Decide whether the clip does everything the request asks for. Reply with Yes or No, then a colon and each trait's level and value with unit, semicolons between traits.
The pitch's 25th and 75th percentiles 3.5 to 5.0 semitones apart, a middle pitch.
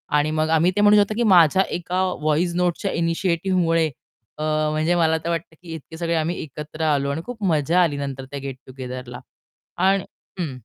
No: average, 2.9 semitones; medium, 160 Hz